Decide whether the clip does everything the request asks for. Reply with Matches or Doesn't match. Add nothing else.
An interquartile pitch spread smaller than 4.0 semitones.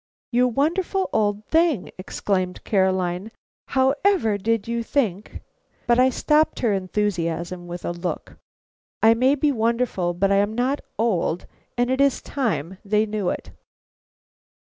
Doesn't match